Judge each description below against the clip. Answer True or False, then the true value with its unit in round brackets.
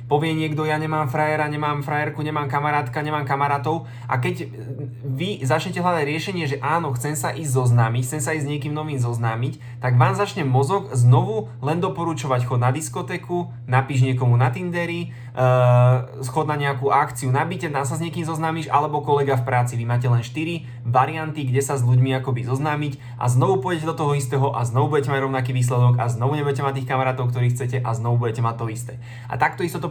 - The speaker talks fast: True (200 wpm)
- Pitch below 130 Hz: False (135 Hz)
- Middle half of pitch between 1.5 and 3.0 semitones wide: False (3.4 semitones)